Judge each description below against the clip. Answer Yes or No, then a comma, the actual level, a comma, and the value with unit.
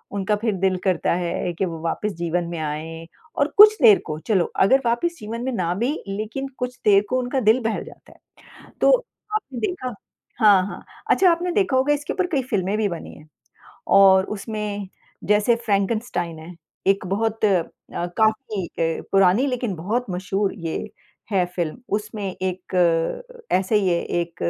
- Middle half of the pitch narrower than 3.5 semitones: No, average, 5.1 semitones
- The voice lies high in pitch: Yes, high, 205 Hz